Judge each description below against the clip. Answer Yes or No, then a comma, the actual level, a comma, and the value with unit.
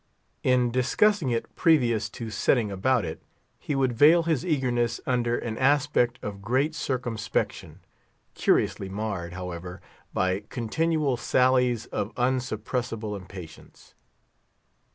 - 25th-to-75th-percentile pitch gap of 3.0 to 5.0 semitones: Yes, average, 3.8 semitones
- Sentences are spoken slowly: Yes, slow, 110 wpm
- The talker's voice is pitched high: No, low, 120 Hz